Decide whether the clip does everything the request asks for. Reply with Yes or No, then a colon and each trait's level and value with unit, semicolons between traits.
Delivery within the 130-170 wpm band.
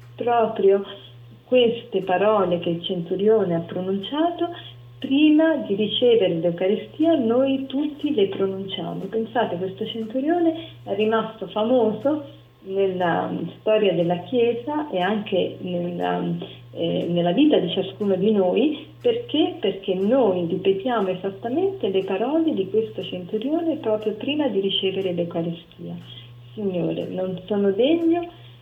No: slow, 115 wpm